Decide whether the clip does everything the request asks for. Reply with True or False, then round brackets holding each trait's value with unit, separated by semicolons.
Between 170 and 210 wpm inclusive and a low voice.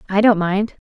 False (205 wpm; 200 Hz)